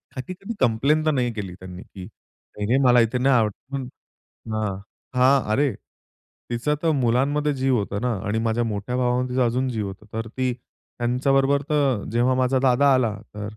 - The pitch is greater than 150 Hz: No, low, 125 Hz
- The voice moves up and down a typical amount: Yes, average, 3.2 semitones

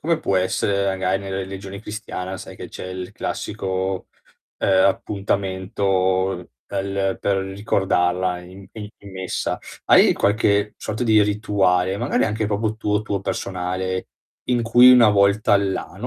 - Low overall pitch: Yes, low, 100 Hz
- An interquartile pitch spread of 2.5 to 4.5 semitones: No, narrow, 1.7 semitones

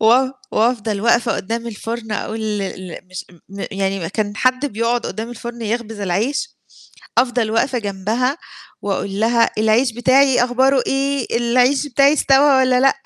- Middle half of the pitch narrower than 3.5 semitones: Yes, average, 3.1 semitones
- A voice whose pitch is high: Yes, high, 235 Hz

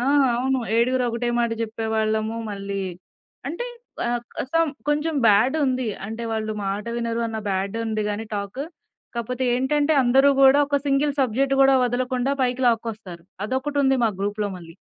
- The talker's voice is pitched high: Yes, high, 235 Hz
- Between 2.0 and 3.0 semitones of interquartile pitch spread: No, average, 3.6 semitones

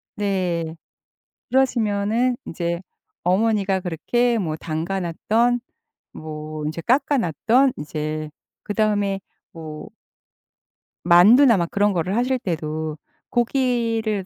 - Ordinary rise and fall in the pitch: No, wide, 6.0 semitones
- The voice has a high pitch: Yes, high, 195 Hz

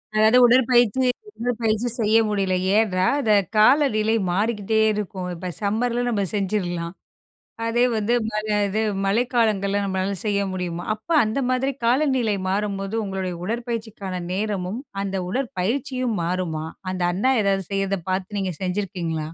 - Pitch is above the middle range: Yes, high, 210 Hz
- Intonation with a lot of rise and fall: No, average, 3.5 semitones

